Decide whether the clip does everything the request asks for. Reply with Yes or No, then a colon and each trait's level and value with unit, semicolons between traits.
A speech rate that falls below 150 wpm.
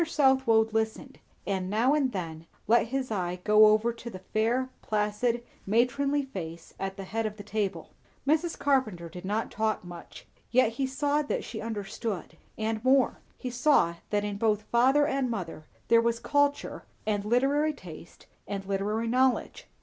No: average, 165 wpm